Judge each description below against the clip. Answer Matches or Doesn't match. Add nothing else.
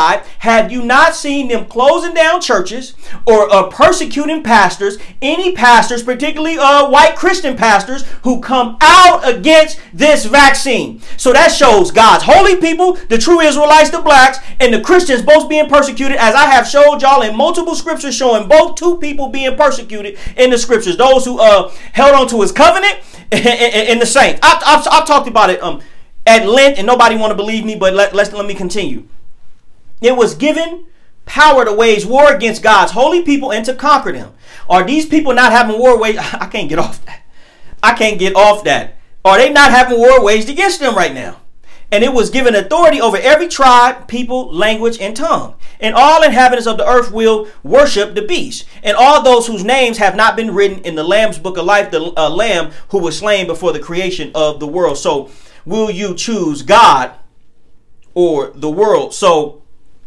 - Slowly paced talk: Doesn't match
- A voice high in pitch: Matches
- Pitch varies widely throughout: Matches